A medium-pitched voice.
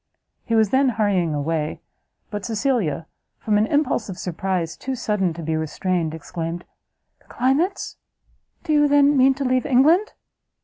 No: high, 215 Hz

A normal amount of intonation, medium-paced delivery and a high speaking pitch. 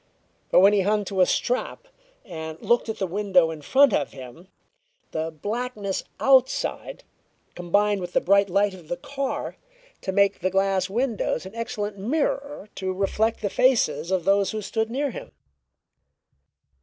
Yes: average, 3.6 semitones; average, 170 wpm; high, 200 Hz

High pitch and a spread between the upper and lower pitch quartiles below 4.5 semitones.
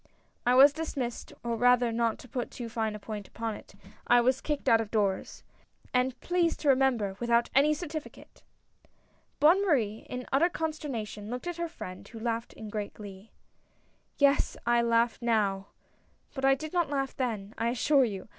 Yes: high, 240 Hz; average, 4.1 semitones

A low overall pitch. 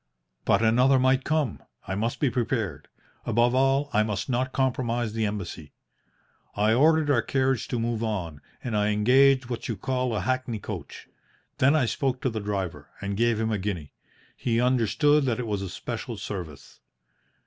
Yes: low, 115 Hz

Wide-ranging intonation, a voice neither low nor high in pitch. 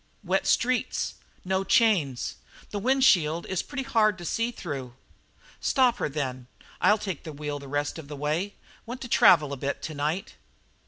Yes: wide, 7.1 semitones; medium, 175 Hz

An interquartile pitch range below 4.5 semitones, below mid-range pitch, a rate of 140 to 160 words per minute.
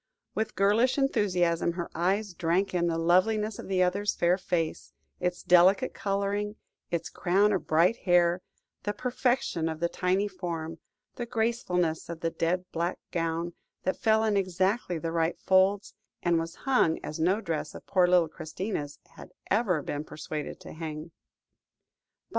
No: average, 3.4 semitones; medium, 180 Hz; average, 155 wpm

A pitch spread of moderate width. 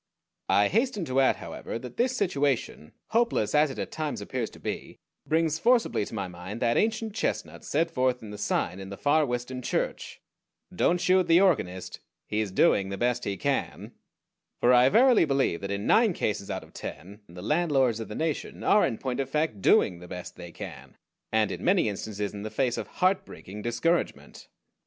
No: wide, 8.3 semitones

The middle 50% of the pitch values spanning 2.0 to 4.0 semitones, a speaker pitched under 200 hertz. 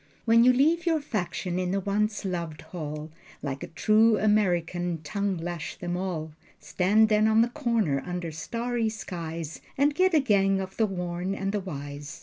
No: average, 4.4 semitones; high, 190 Hz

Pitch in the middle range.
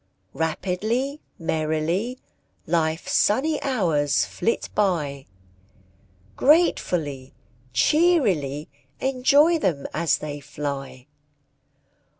Yes: medium, 170 Hz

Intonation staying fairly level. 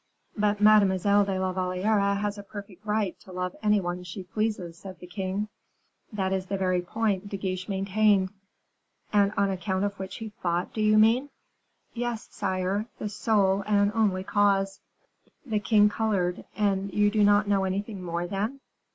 Yes: narrow, 2.0 semitones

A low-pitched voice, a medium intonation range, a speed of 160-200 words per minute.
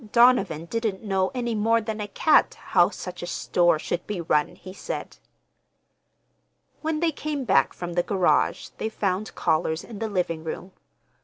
No: high, 195 Hz; average, 4.6 semitones; average, 165 wpm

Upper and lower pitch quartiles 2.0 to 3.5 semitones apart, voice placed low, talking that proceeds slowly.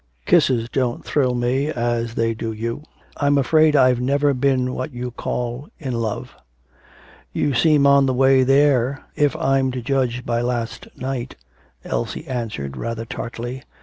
No: narrow, 2.6 semitones; low, 125 Hz; average, 150 wpm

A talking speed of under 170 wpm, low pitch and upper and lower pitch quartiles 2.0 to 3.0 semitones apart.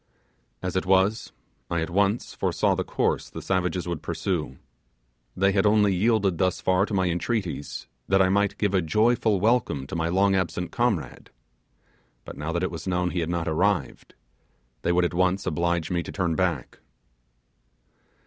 No: average, 175 wpm; very low, 95 Hz; narrow, 2.5 semitones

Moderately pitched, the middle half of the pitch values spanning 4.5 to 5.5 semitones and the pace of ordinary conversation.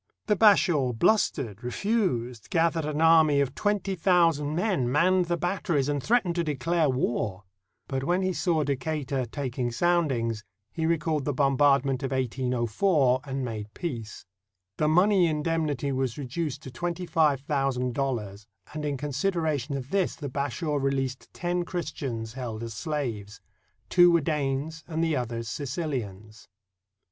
Yes: medium, 145 Hz; average, 4.8 semitones; average, 150 wpm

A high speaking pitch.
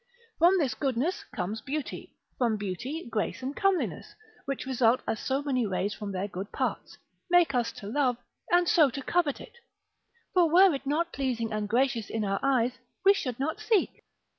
Yes: very high, 265 Hz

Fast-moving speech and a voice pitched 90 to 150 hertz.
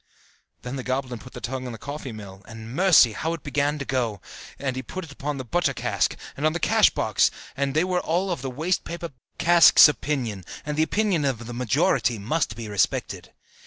Yes: fast, 210 wpm; low, 135 Hz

